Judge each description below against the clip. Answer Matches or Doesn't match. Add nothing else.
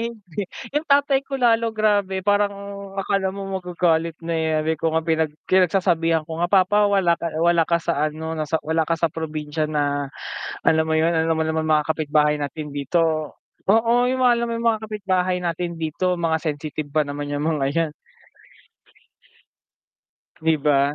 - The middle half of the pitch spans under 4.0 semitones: Matches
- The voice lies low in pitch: Doesn't match